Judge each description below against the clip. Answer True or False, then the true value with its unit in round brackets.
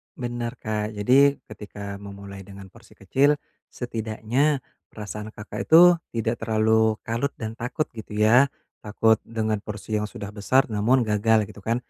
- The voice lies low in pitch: True (110 Hz)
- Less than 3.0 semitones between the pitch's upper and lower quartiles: True (2.4 semitones)